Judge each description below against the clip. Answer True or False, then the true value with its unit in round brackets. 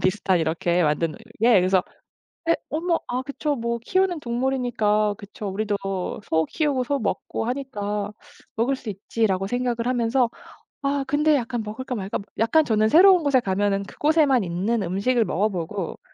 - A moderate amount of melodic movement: True (5.0 semitones)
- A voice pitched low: False (230 Hz)